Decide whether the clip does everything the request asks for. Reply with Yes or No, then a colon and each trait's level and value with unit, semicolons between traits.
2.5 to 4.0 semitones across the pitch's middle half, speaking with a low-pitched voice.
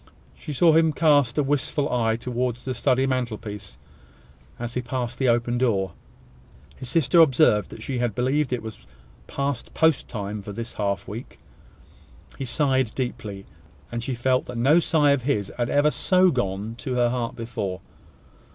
Yes: average, 3.5 semitones; low, 125 Hz